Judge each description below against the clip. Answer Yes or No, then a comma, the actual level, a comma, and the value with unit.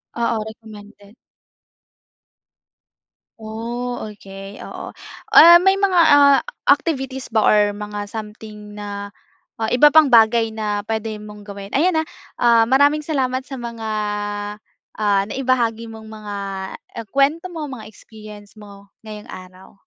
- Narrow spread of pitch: No, average, 3.9 semitones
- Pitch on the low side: No, high, 220 Hz